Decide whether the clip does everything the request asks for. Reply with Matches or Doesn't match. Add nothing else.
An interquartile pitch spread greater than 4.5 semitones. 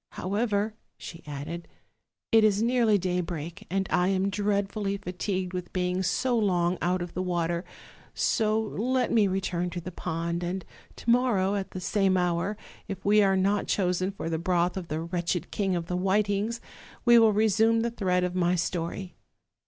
Doesn't match